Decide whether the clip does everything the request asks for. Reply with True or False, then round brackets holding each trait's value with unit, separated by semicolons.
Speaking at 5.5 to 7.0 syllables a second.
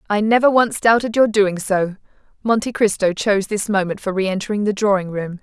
True (5.7 syllables/s)